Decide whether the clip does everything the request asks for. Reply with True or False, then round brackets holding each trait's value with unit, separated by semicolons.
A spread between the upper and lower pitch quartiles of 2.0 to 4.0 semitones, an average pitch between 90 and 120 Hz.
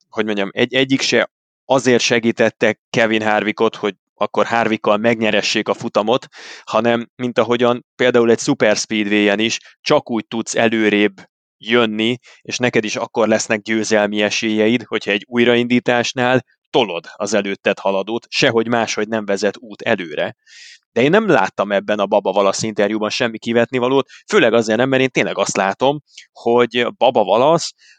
True (2.4 semitones; 115 Hz)